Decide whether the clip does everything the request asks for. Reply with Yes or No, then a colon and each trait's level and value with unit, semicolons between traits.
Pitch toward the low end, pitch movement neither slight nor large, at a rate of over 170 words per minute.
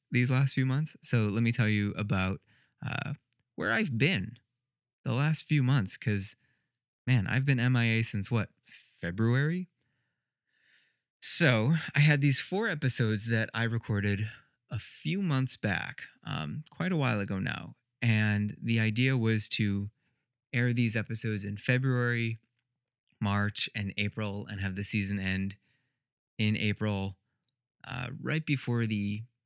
No: low, 120 Hz; average, 3.8 semitones; average, 140 wpm